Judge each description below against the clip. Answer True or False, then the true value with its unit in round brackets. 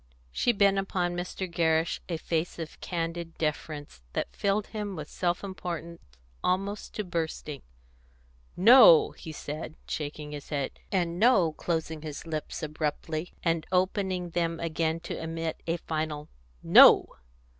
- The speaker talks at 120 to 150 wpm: True (135 wpm)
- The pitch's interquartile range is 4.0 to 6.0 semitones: False (2.5 semitones)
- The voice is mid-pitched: True (165 Hz)